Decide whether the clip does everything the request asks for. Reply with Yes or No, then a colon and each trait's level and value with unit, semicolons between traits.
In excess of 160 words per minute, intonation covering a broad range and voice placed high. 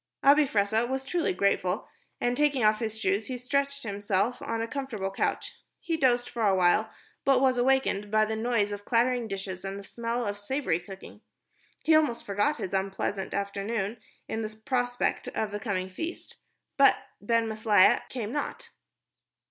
No: average, 170 wpm; average, 4.0 semitones; high, 220 Hz